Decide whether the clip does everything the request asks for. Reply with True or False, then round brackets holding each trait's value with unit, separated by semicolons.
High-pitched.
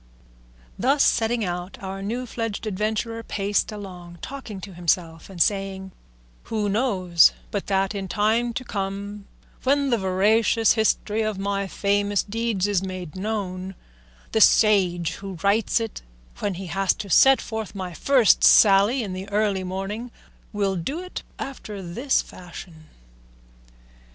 True (200 Hz)